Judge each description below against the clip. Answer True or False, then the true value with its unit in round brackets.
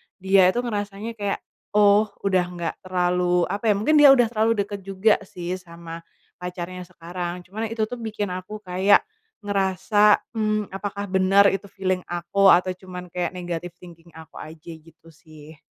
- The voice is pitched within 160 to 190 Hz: True (185 Hz)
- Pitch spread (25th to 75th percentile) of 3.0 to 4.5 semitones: False (2.6 semitones)